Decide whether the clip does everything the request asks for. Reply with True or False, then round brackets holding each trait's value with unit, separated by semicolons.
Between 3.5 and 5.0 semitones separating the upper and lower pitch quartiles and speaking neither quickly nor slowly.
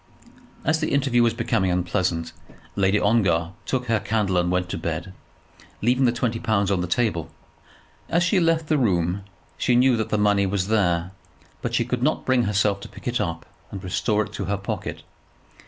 True (4.7 semitones; 195 wpm)